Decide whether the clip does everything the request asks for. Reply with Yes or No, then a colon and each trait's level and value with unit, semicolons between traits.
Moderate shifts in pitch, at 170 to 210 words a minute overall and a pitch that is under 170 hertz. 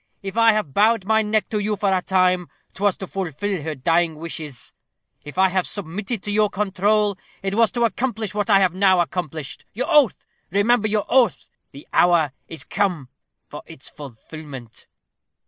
No: average, 4.1 semitones; average, 175 wpm; high, 195 Hz